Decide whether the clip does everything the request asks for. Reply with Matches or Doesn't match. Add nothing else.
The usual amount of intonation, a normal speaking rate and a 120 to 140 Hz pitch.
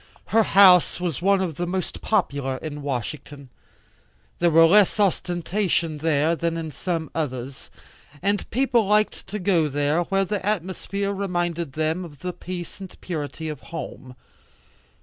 Doesn't match